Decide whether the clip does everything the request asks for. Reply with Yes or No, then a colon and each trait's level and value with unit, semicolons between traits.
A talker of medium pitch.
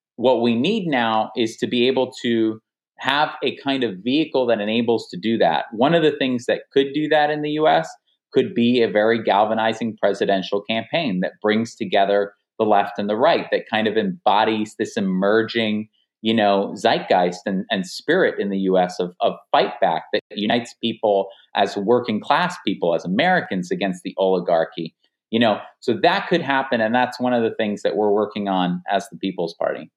No: low, 110 Hz